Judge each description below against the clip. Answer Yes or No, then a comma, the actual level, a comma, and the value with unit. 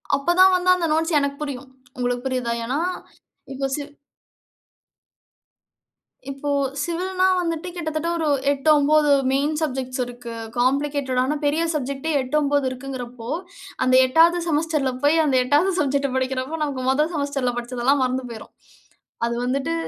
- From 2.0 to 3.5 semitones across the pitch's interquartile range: Yes, average, 3.2 semitones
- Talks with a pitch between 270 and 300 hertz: Yes, very high, 280 Hz